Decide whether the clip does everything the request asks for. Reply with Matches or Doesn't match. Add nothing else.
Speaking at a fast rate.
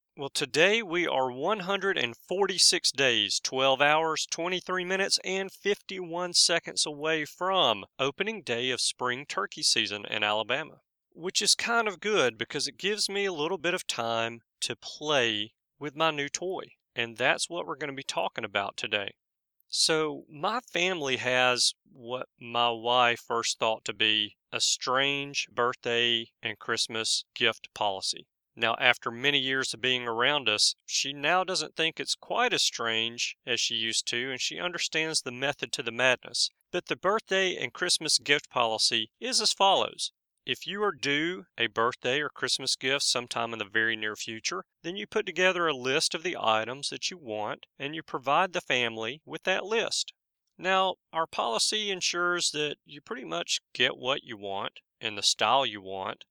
Doesn't match